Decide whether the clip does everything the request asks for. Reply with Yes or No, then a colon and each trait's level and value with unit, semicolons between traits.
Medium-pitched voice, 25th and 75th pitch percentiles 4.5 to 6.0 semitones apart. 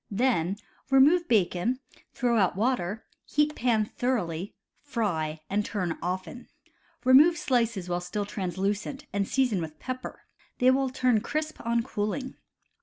No: high, 225 Hz; wide, 5.5 semitones